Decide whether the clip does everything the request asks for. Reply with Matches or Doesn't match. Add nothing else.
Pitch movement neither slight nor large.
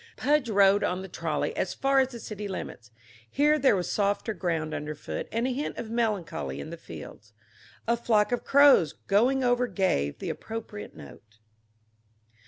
Doesn't match